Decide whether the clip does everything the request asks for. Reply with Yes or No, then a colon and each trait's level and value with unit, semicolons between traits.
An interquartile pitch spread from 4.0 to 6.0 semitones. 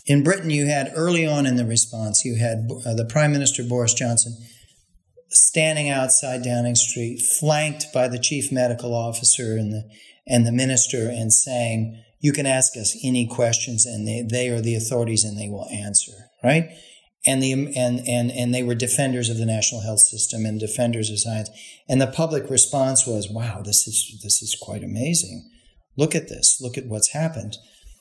No: average, 3.0 semitones